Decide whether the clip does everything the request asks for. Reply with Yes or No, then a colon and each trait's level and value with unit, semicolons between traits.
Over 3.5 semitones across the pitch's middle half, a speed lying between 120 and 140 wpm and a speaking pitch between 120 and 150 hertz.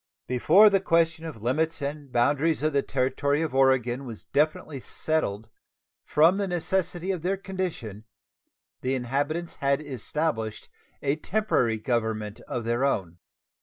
Yes: average, 5.2 semitones; slow, 135 wpm; medium, 140 Hz